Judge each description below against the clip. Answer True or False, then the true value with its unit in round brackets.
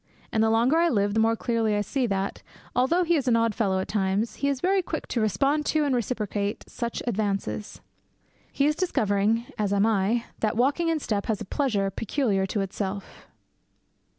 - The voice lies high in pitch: True (225 Hz)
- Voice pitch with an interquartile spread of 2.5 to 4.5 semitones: False (4.9 semitones)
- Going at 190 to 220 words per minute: True (195 wpm)